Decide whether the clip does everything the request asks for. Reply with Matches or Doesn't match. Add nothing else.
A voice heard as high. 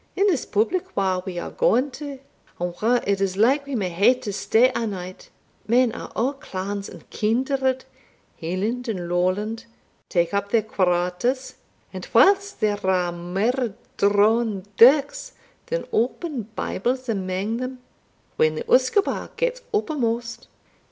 Matches